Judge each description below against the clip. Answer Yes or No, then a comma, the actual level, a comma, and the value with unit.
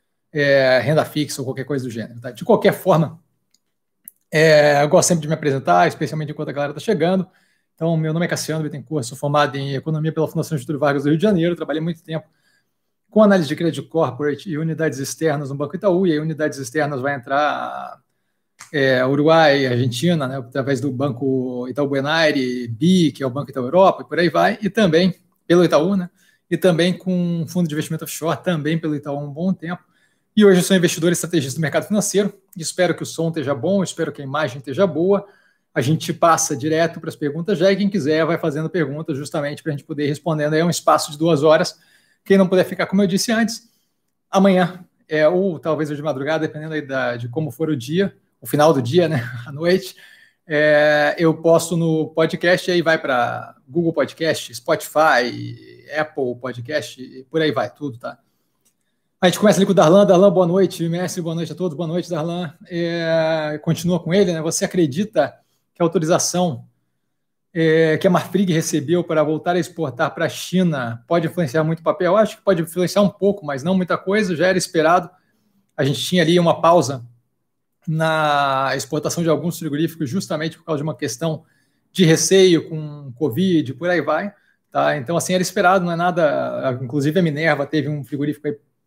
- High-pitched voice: No, medium, 160 Hz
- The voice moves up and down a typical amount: Yes, average, 3.3 semitones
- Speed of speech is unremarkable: No, fast, 205 wpm